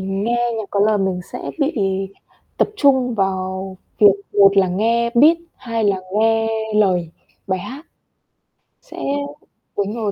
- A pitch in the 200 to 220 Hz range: Yes, high, 210 Hz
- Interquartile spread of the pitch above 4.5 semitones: No, average, 3.4 semitones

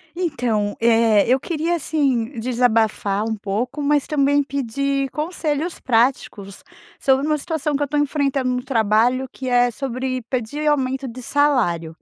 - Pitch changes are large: No, average, 3.9 semitones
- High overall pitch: Yes, very high, 260 Hz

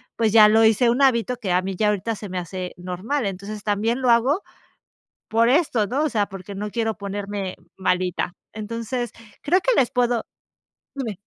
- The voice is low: No, high, 215 Hz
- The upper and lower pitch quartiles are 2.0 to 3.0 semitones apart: No, average, 3.5 semitones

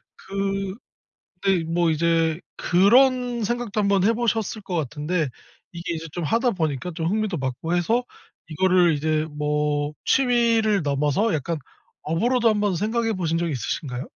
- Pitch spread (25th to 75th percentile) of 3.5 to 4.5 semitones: No, wide, 5.5 semitones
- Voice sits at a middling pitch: Yes, medium, 180 Hz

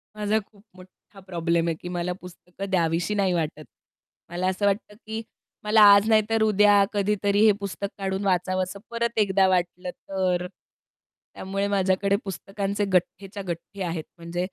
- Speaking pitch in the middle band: No, high, 195 Hz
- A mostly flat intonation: Yes, narrow, 2.2 semitones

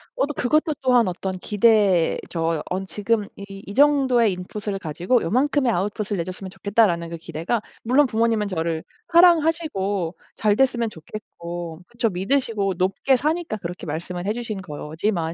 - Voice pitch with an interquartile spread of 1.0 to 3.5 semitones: No, average, 5.2 semitones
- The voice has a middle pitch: No, high, 205 Hz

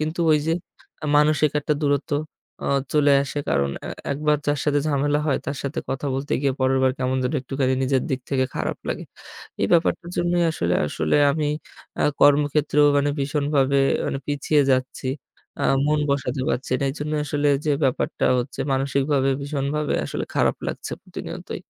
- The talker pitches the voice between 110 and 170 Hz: Yes, medium, 140 Hz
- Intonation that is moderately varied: No, narrow, 1.9 semitones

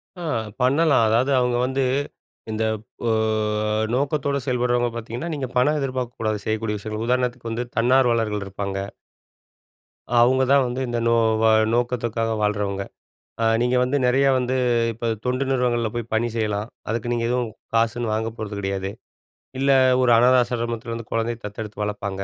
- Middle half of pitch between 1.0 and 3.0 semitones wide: Yes, narrow, 2.4 semitones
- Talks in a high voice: No, low, 120 Hz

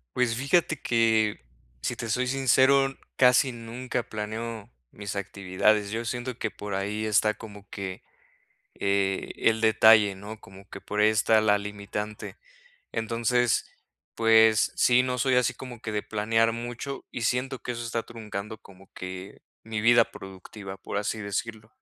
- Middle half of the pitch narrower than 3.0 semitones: Yes, narrow, 2.6 semitones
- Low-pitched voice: Yes, low, 110 Hz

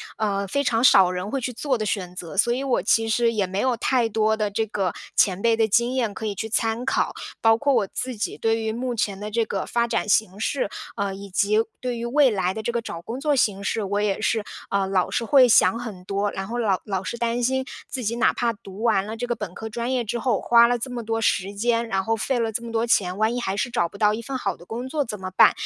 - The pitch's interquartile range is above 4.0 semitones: No, average, 3.1 semitones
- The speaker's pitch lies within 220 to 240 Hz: Yes, high, 225 Hz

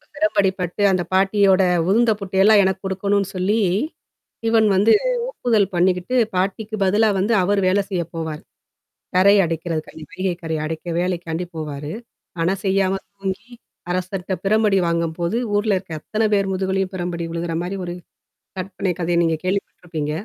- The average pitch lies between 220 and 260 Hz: No, high, 190 Hz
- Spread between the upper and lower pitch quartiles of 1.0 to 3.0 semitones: Yes, narrow, 2.5 semitones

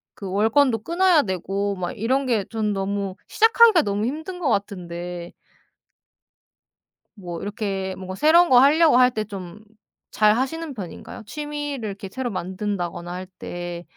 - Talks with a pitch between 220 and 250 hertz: No, high, 210 Hz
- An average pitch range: No, wide, 6.6 semitones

